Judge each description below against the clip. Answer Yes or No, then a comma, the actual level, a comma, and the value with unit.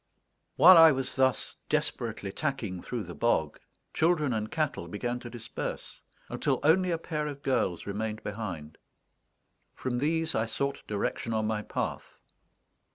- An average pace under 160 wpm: Yes, average, 145 wpm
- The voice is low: Yes, low, 120 Hz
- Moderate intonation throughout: No, wide, 6.0 semitones